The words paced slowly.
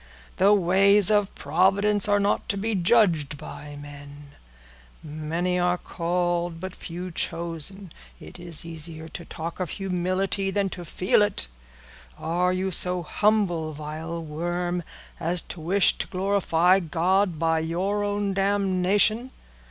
Yes: slow, 130 wpm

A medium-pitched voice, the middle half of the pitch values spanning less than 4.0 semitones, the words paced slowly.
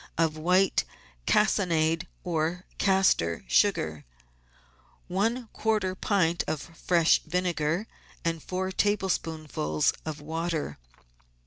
Yes: medium, 170 Hz; average, 3.2 semitones; slow, 90 wpm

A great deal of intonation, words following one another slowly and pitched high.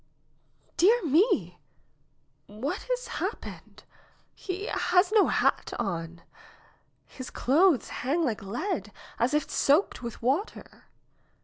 Yes: wide, 8.2 semitones; slow, 105 wpm; very high, 295 Hz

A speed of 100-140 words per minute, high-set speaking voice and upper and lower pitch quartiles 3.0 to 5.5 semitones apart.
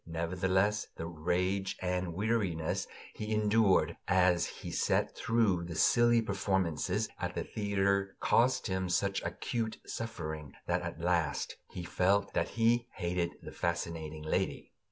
No: slow, 135 wpm; very low, 95 Hz; average, 3.6 semitones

